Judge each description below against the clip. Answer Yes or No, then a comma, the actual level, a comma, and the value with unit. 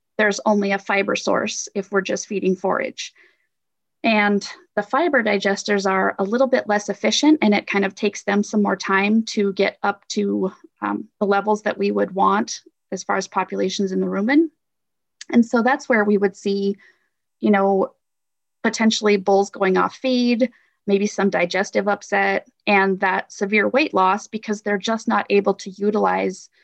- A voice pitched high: Yes, high, 205 Hz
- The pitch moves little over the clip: Yes, narrow, 2.1 semitones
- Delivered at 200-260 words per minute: No, average, 175 wpm